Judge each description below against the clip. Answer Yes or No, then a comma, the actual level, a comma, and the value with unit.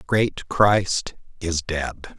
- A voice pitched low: Yes, very low, 90 Hz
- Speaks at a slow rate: Yes, slow, 110 wpm